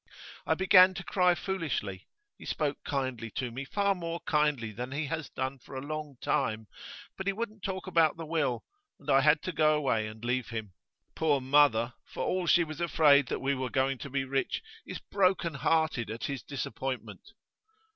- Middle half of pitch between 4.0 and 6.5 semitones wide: Yes, average, 4.4 semitones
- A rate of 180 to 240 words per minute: Yes, average, 190 wpm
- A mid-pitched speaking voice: Yes, medium, 145 Hz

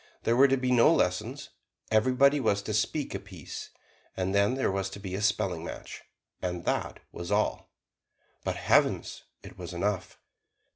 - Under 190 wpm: Yes, average, 165 wpm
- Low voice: Yes, low, 105 Hz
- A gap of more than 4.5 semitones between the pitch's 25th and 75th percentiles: Yes, average, 5.0 semitones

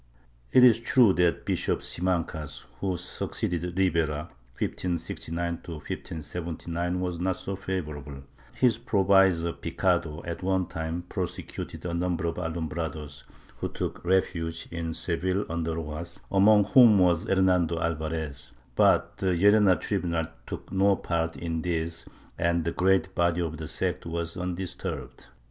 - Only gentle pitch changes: Yes, narrow, 2.3 semitones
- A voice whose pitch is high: No, very low, 85 Hz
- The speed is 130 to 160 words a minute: Yes, average, 140 wpm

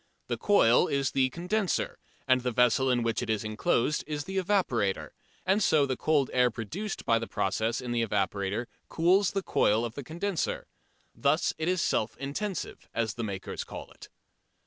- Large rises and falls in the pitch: Yes, wide, 7.1 semitones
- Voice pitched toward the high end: No, low, 130 Hz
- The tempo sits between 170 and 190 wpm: Yes, average, 180 wpm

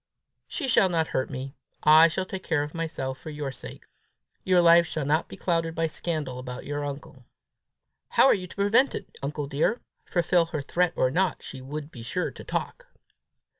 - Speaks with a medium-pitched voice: Yes, medium, 160 Hz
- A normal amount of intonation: Yes, average, 3.9 semitones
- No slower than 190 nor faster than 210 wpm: Yes, average, 195 wpm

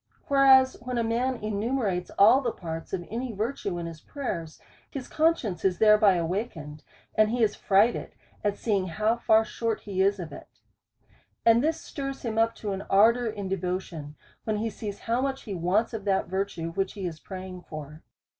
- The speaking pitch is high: Yes, high, 210 Hz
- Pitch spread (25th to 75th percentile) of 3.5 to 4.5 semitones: Yes, average, 4.2 semitones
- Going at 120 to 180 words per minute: No, average, 190 wpm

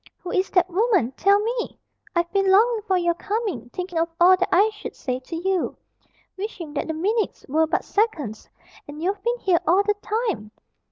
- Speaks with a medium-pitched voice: No, very high, 370 Hz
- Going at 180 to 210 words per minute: Yes, average, 190 wpm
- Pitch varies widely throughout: No, average, 4.0 semitones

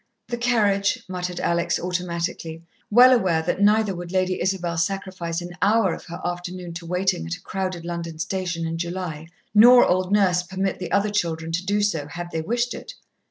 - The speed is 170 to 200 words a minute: Yes, average, 185 wpm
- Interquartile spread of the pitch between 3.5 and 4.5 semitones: No, average, 2.7 semitones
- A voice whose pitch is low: No, medium, 180 Hz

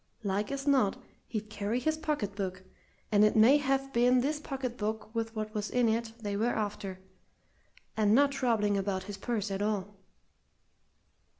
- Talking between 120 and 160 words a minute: No, average, 170 wpm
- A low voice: No, high, 220 Hz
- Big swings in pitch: No, average, 3.5 semitones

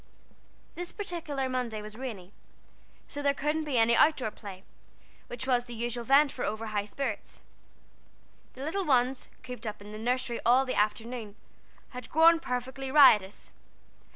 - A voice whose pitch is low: No, very high, 250 Hz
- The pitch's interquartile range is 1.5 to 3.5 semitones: No, average, 4.0 semitones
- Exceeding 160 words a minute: No, average, 155 wpm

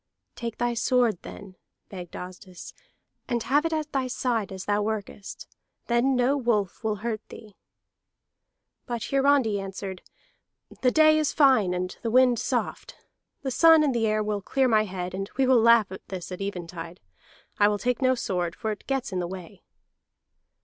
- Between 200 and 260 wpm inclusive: No, average, 175 wpm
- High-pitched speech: Yes, high, 220 Hz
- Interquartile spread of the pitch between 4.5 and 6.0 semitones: Yes, average, 5.0 semitones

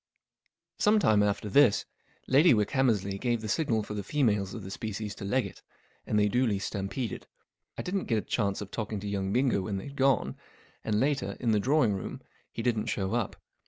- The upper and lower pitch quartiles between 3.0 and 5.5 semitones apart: Yes, average, 4.2 semitones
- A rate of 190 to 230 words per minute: Yes, average, 200 wpm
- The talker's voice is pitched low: Yes, low, 110 Hz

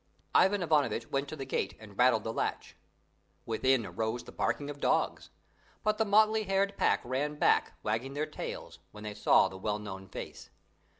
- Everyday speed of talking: Yes, average, 185 wpm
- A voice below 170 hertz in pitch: Yes, low, 135 Hz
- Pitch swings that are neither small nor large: No, wide, 6.1 semitones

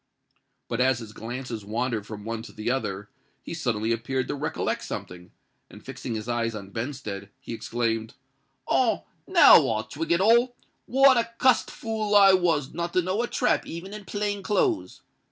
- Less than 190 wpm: Yes, average, 170 wpm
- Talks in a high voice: No, low, 130 Hz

